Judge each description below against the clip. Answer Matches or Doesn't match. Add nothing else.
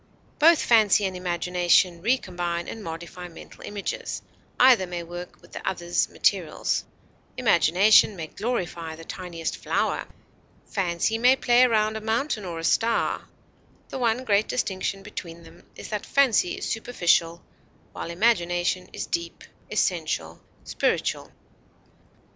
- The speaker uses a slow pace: Matches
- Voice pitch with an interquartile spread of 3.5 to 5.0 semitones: Matches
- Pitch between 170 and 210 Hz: Matches